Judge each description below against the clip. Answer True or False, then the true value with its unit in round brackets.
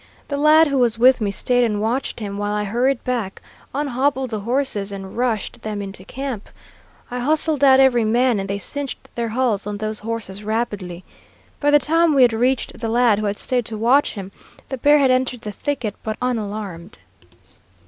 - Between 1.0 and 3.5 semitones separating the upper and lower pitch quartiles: False (4.1 semitones)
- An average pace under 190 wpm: False (195 wpm)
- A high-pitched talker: True (235 Hz)